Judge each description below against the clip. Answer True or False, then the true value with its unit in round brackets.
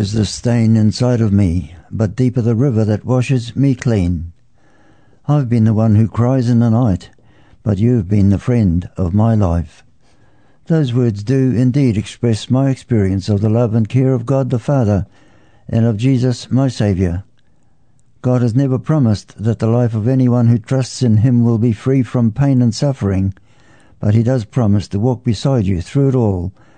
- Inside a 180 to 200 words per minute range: True (185 wpm)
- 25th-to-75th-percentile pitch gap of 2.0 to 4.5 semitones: True (3.5 semitones)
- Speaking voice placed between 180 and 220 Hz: False (115 Hz)